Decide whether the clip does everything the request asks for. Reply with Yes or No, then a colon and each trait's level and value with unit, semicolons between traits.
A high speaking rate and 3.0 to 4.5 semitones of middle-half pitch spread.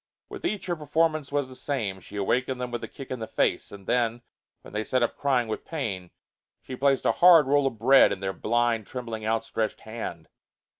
Yes: fast, 210 wpm; average, 3.9 semitones